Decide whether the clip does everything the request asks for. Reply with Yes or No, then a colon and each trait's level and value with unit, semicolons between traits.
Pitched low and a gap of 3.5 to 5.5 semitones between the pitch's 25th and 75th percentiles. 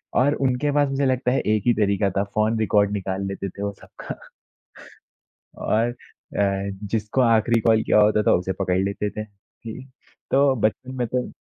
Yes: low, 110 Hz; average, 3.8 semitones